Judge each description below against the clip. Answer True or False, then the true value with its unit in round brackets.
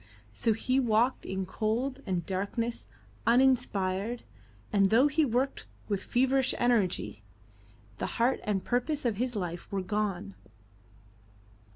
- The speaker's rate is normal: False (125 wpm)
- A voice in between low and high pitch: False (225 Hz)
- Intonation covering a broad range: False (4.6 semitones)